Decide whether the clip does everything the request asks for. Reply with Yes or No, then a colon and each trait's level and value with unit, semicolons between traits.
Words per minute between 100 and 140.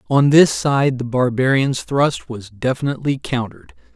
Yes: slow, 135 wpm